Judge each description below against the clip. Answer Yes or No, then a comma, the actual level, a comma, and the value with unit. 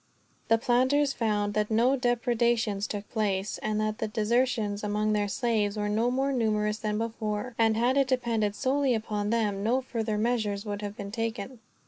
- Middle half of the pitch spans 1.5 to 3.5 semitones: Yes, narrow, 2.5 semitones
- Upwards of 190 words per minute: No, average, 175 wpm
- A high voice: Yes, high, 220 Hz